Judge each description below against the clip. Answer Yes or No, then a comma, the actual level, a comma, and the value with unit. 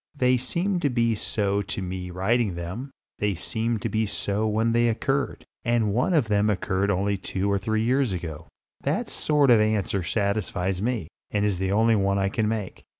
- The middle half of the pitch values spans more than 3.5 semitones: No, average, 3.2 semitones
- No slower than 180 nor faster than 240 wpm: Yes, average, 195 wpm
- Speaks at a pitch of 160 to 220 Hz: No, low, 105 Hz